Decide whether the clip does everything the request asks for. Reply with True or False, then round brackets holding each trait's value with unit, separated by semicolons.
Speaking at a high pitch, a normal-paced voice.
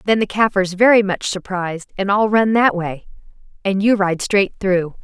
True (195 Hz; 190 wpm)